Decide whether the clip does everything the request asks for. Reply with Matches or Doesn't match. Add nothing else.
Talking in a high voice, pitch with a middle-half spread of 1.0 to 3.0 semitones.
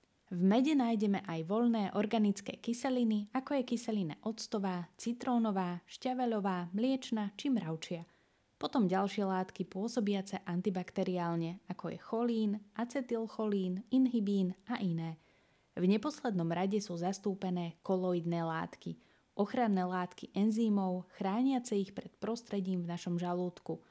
Doesn't match